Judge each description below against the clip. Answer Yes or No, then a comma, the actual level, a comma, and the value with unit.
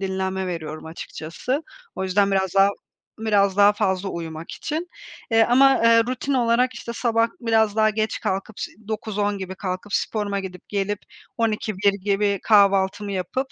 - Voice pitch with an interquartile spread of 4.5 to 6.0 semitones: No, average, 2.8 semitones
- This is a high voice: Yes, high, 205 Hz